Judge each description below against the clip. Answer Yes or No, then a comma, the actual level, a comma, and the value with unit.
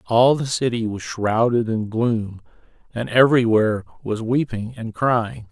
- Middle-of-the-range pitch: No, low, 115 Hz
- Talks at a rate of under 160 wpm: Yes, average, 140 wpm